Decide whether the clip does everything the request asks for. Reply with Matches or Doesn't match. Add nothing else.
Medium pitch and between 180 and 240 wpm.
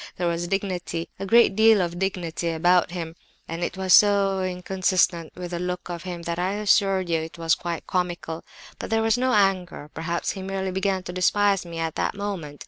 Matches